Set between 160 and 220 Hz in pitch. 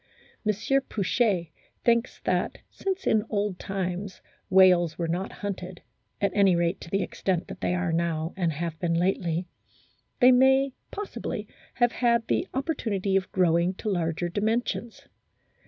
Yes: high, 190 Hz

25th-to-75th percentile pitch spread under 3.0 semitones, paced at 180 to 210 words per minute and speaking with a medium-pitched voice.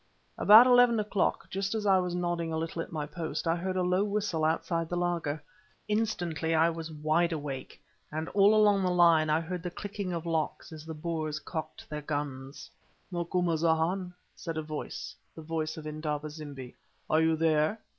Yes: narrow, 2.6 semitones; average, 185 wpm; medium, 165 Hz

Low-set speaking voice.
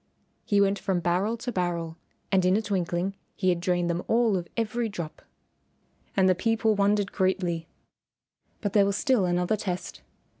No: high, 190 Hz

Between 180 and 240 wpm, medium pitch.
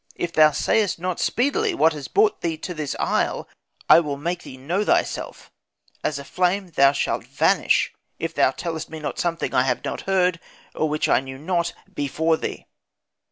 Yes: average, 185 wpm; medium, 165 Hz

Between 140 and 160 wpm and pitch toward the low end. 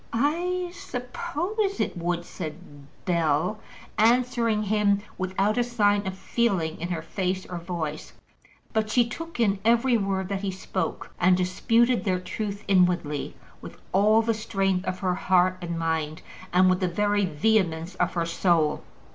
No: average, 155 wpm; high, 190 Hz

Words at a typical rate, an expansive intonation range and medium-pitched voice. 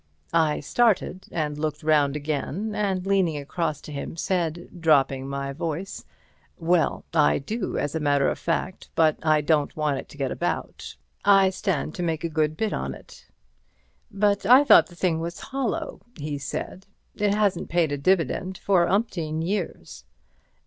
No: average, 165 wpm; average, 4.2 semitones; medium, 165 Hz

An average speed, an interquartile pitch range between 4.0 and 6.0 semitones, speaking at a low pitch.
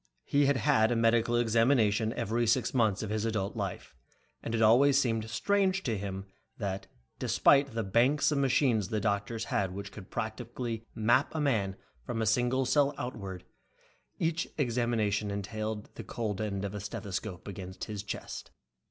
No: average, 170 wpm; average, 3.4 semitones; low, 115 Hz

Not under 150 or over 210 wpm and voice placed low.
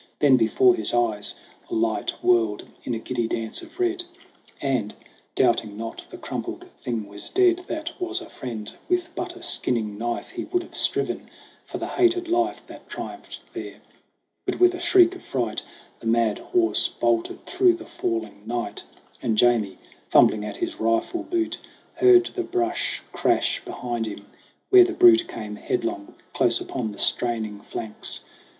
Yes: average, 165 wpm; low, 130 Hz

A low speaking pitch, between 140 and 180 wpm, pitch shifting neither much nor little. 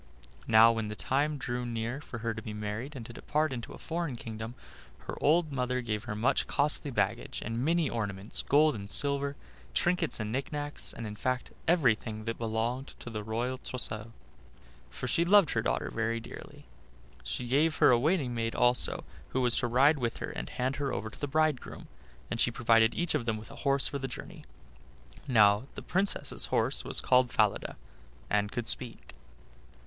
No: low, 120 Hz; average, 190 wpm; average, 3.9 semitones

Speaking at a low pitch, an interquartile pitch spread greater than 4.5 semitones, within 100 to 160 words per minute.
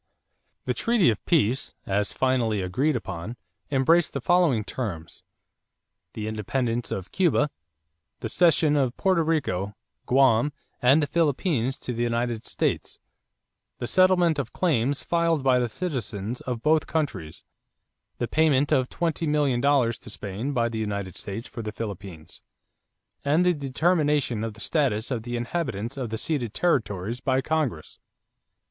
Yes: low, 130 Hz; wide, 5.4 semitones; average, 150 wpm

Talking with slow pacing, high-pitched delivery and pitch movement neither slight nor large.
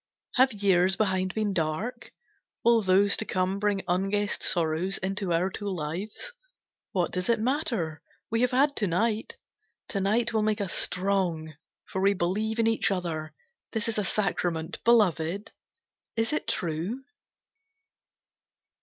No: average, 145 wpm; high, 195 Hz; average, 3.7 semitones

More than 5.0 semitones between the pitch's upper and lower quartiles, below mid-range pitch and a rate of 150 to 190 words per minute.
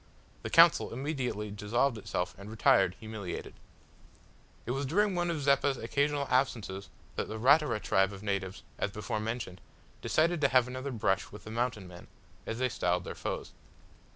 Yes: wide, 5.6 semitones; low, 115 Hz; average, 165 wpm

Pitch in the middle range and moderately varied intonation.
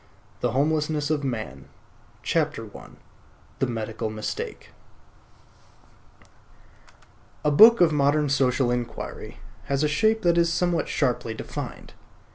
Yes: medium, 145 Hz; average, 4.5 semitones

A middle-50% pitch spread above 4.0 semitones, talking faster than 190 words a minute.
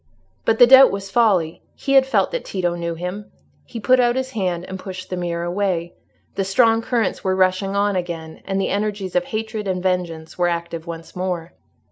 No: average, 3.7 semitones; average, 200 wpm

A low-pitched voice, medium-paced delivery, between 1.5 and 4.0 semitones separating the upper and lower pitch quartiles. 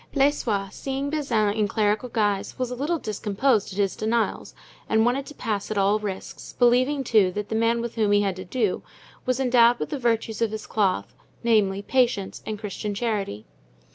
No: high, 220 Hz; average, 190 wpm; average, 3.3 semitones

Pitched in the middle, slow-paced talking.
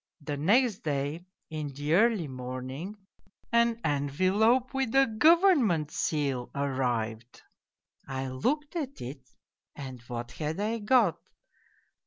Yes: medium, 155 Hz; slow, 115 wpm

